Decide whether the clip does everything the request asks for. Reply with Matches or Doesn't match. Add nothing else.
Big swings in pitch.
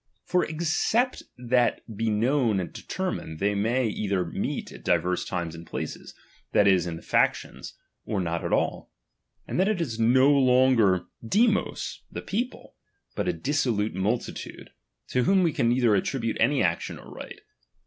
Matches